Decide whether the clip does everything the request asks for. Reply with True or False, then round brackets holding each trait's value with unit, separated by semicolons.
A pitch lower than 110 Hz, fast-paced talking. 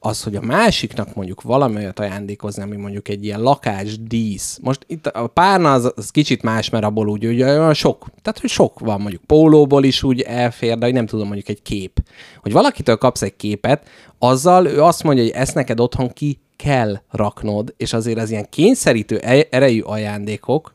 False (115 Hz; 190 wpm)